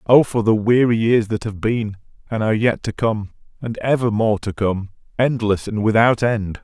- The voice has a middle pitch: No, low, 110 Hz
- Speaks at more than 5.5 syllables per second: No, 5.0 syllables/s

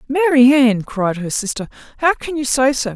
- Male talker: No, female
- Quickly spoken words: No, average, 180 wpm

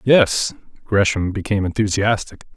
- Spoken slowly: Yes, slow, 95 wpm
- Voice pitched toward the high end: No, low, 100 Hz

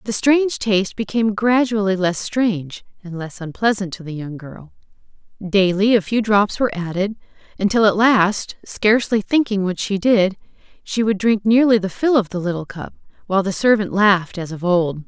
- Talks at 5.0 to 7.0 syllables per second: Yes, 5.2 syllables/s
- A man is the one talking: No, female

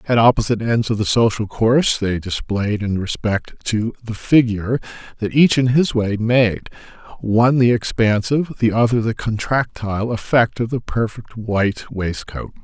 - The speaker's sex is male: Yes, male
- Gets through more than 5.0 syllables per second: No, 4.8 syllables/s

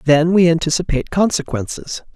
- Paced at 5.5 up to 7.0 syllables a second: Yes, 5.7 syllables/s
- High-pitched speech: No, medium, 165 Hz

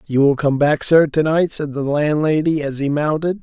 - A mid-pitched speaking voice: Yes, medium, 150 Hz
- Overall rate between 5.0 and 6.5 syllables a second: No, 4.8 syllables/s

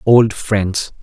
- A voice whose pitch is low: Yes, low, 105 Hz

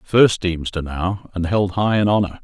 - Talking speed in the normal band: Yes, average, 195 wpm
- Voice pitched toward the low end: Yes, very low, 95 Hz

